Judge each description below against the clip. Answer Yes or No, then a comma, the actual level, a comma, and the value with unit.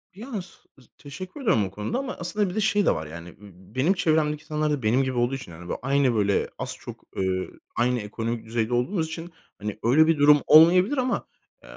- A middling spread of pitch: No, wide, 7.3 semitones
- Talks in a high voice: No, medium, 140 Hz